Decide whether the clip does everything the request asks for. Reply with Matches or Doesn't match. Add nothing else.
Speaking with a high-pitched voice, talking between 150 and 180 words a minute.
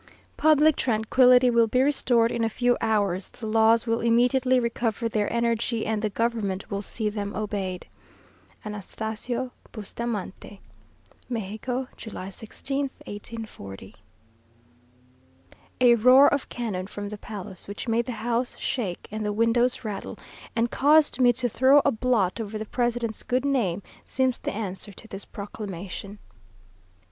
Doesn't match